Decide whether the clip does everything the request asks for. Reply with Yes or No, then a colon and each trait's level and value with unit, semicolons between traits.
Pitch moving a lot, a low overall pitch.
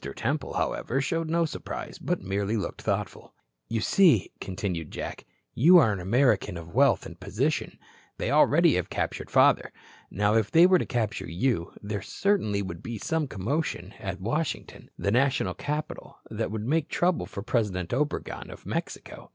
Yes: wide, 7.1 semitones; low, 115 Hz